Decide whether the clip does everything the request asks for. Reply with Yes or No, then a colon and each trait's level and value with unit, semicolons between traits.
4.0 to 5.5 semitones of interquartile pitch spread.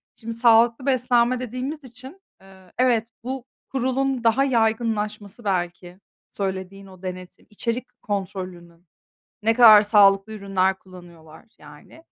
Yes: average, 4.5 semitones